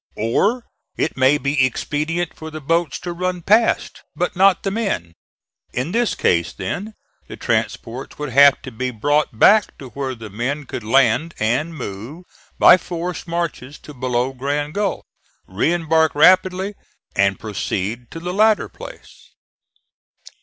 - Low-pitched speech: No, medium, 150 Hz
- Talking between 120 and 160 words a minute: Yes, average, 150 wpm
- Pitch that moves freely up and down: Yes, wide, 6.0 semitones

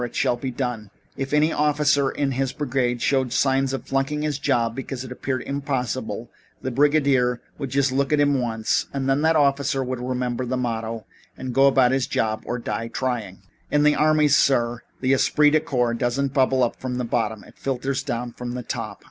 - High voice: No, low, 130 Hz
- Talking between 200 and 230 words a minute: Yes, fast, 205 wpm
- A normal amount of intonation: No, narrow, 2.3 semitones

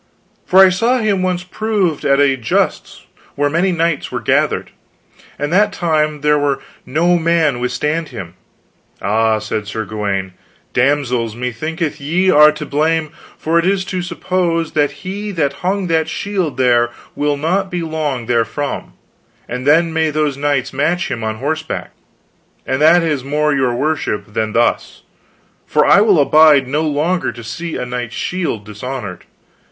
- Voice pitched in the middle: Yes, medium, 150 Hz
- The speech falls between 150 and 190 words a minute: Yes, average, 160 wpm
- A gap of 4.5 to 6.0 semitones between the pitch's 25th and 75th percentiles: Yes, average, 4.8 semitones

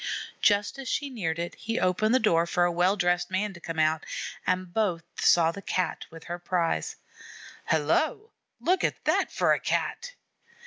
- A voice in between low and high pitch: Yes, medium, 180 Hz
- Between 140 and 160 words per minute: No, average, 180 wpm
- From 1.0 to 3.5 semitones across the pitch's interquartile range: No, average, 4.1 semitones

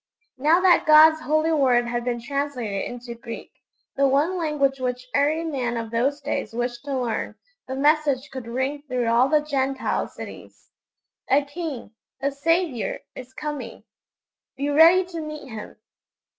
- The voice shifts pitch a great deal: No, average, 3.7 semitones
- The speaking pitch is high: Yes, very high, 275 Hz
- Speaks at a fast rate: No, average, 155 wpm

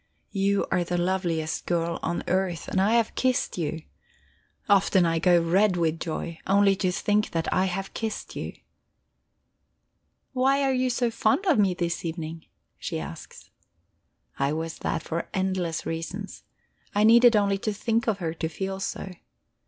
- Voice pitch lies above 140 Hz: Yes, high, 190 Hz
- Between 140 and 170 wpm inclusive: Yes, average, 160 wpm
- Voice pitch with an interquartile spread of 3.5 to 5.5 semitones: Yes, average, 3.9 semitones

